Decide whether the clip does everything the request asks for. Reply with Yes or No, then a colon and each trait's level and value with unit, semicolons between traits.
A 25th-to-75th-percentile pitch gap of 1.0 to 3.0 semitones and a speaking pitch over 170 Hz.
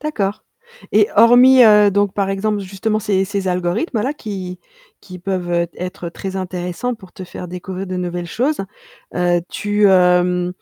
Yes: average, 2.7 semitones; high, 190 Hz